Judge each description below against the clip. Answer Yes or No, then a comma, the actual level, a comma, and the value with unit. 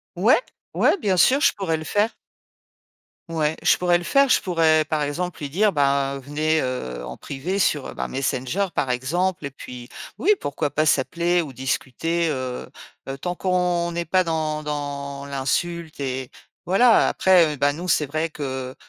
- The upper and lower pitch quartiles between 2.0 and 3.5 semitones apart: No, average, 4.2 semitones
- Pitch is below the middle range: No, medium, 155 Hz